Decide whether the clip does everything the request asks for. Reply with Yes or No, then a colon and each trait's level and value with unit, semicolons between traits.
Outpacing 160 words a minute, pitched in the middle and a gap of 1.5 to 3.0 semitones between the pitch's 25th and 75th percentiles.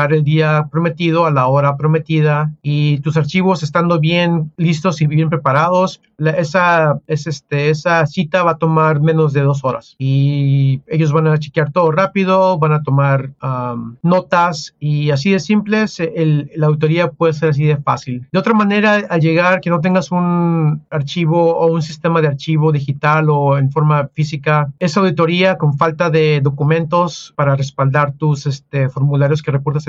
Yes: average, 175 wpm; medium, 155 Hz; average, 2.7 semitones